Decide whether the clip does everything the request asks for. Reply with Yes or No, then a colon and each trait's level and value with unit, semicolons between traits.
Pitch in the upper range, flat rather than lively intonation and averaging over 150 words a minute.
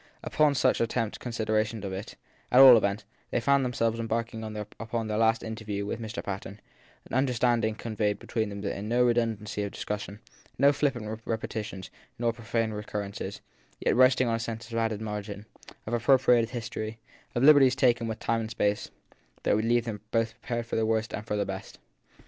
No: low, 115 Hz; narrow, 2.0 semitones; average, 195 wpm